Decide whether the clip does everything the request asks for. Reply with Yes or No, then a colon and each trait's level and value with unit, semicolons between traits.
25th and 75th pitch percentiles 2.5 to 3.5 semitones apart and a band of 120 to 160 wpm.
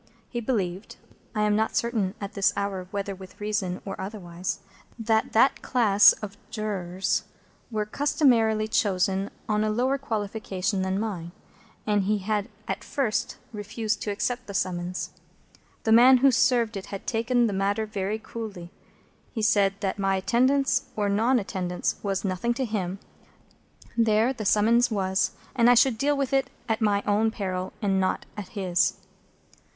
Yes: average, 3.0 semitones; average, 155 wpm